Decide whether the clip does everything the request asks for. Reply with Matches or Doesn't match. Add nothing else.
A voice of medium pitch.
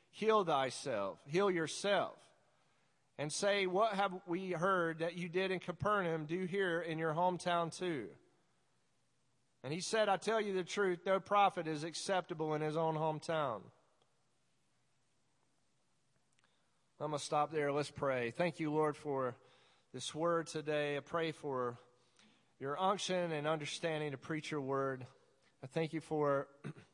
Matches